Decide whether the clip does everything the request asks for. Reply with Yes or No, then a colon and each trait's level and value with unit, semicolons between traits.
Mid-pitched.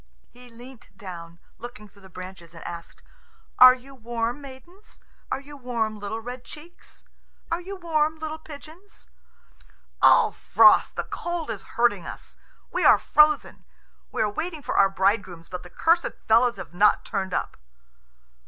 No: high, 240 Hz